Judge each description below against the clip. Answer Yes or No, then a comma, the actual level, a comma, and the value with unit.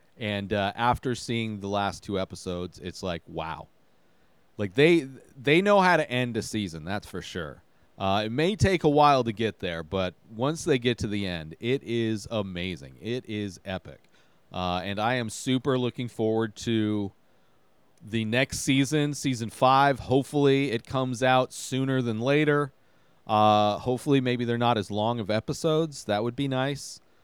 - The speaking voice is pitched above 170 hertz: No, low, 115 Hz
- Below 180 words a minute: Yes, average, 170 wpm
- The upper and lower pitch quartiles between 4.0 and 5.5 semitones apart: Yes, average, 4.7 semitones